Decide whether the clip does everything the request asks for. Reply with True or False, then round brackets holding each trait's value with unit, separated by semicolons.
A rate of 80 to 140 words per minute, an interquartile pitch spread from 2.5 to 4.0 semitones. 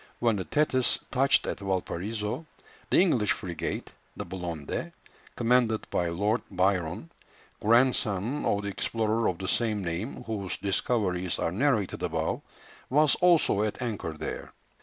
False (135 wpm; 4.7 semitones)